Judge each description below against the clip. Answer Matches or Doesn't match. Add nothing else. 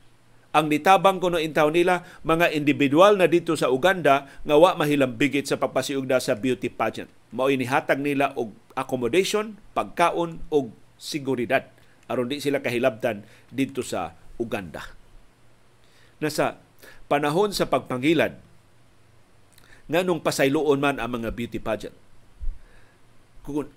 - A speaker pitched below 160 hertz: Matches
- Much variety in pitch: Doesn't match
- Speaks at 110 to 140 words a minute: Matches